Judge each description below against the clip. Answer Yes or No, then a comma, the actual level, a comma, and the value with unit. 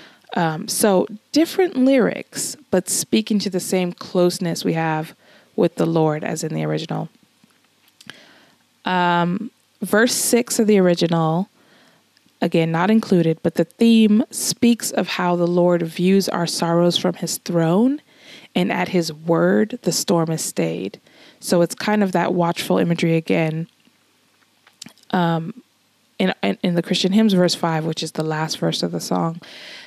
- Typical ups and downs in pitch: Yes, average, 4.1 semitones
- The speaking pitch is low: No, medium, 175 Hz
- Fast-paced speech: No, average, 150 wpm